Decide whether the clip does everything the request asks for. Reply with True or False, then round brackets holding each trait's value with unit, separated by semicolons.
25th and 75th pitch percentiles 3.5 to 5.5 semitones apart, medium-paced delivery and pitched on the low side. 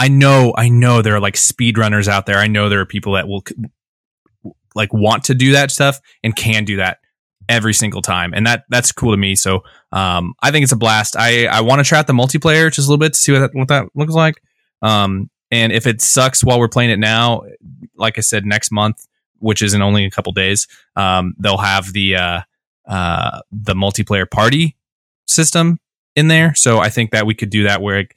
False (4.3 semitones; 230 wpm; 110 Hz)